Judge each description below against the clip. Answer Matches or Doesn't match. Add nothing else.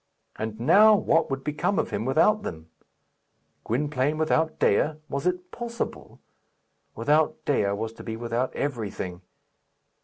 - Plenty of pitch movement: Matches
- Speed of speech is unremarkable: Doesn't match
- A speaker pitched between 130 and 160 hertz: Matches